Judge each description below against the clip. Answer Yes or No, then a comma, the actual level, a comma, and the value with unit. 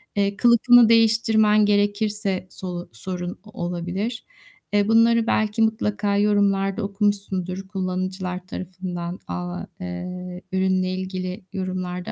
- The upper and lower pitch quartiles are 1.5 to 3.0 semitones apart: Yes, narrow, 2.4 semitones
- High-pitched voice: Yes, high, 195 Hz